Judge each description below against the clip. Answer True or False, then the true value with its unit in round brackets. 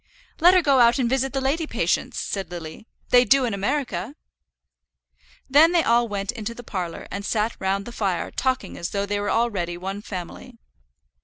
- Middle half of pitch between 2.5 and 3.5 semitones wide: False (5.2 semitones)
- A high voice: True (225 Hz)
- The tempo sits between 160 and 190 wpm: True (185 wpm)